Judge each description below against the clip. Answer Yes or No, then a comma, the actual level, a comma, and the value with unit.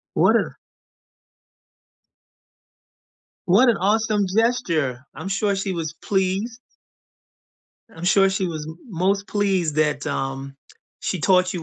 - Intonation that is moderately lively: Yes, average, 4.1 semitones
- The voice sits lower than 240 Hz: Yes, high, 190 Hz